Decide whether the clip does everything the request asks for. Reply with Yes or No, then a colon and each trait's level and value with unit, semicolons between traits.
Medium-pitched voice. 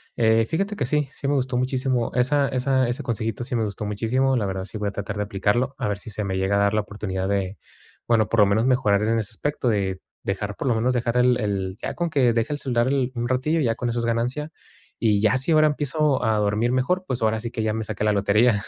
No: low, 115 Hz